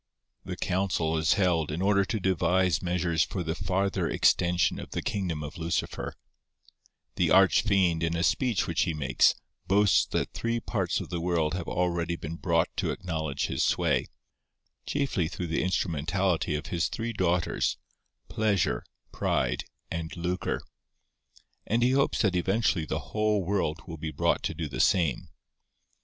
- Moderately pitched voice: No, very low, 90 Hz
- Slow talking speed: No, average, 155 wpm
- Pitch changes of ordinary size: Yes, average, 3.1 semitones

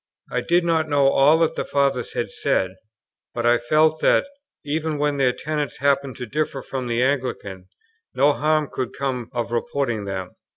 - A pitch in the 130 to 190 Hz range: Yes, low, 135 Hz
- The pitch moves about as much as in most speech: Yes, average, 3.8 semitones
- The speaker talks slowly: No, average, 175 wpm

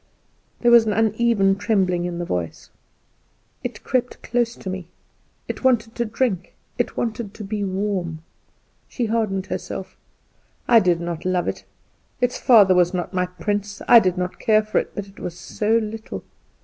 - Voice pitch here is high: Yes, high, 205 Hz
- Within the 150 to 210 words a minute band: Yes, average, 170 wpm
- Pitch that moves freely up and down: No, average, 3.8 semitones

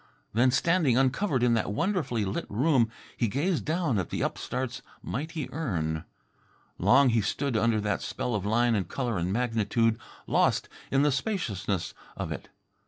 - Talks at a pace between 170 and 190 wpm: No, average, 160 wpm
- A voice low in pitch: Yes, low, 120 Hz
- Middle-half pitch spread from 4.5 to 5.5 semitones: Yes, average, 5.0 semitones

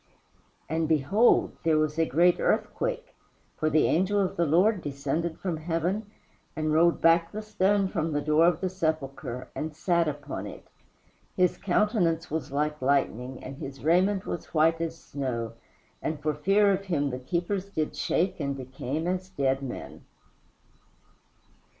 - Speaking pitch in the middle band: Yes, medium, 160 Hz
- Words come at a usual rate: Yes, average, 155 wpm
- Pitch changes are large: No, average, 4.0 semitones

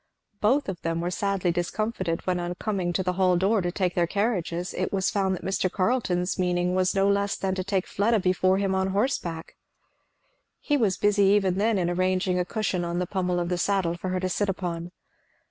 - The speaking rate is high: Yes, fast, 215 wpm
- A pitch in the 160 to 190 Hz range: Yes, medium, 185 Hz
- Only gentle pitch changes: Yes, narrow, 2.0 semitones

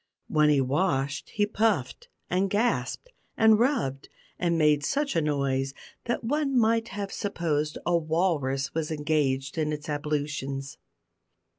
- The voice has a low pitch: No, medium, 155 Hz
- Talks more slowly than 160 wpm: Yes, slow, 135 wpm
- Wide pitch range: Yes, wide, 6.4 semitones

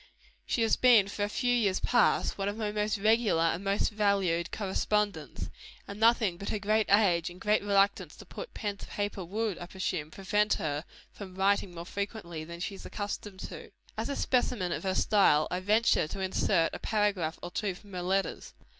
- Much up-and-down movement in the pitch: No, average, 2.7 semitones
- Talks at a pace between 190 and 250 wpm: Yes, average, 200 wpm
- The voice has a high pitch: Yes, high, 200 Hz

